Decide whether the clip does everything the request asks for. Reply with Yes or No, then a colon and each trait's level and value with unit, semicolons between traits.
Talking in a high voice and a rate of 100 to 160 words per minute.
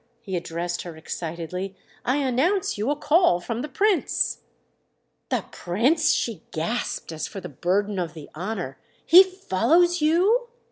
Yes: high, 220 Hz; average, 140 wpm